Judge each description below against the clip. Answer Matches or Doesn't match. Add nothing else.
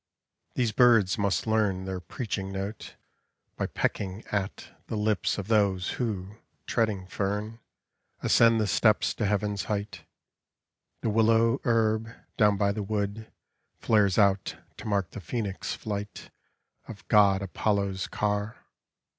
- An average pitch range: Doesn't match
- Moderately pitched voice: Doesn't match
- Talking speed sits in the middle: Doesn't match